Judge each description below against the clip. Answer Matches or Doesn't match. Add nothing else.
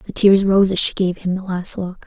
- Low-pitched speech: Doesn't match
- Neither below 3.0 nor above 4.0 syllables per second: Doesn't match